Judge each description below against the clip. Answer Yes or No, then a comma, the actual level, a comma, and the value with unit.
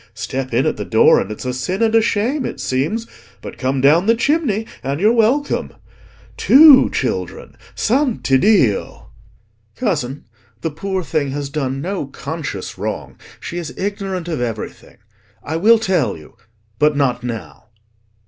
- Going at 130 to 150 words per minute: Yes, average, 145 wpm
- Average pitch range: No, wide, 8.8 semitones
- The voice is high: No, medium, 160 Hz